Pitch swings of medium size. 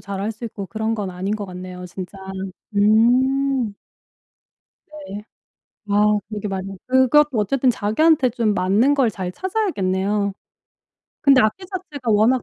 Yes: average, 4.6 semitones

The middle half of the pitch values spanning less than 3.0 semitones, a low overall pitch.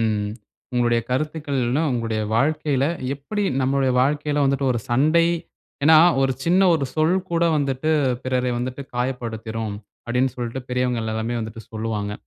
No: average, 3.8 semitones; low, 130 Hz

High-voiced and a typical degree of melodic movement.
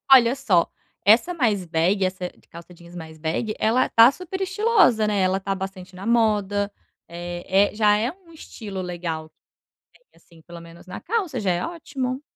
No: high, 205 Hz; wide, 6.1 semitones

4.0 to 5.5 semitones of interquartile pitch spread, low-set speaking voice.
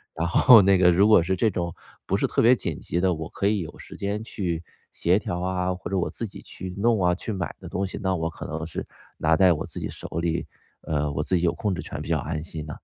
No: average, 2.9 semitones; very low, 90 Hz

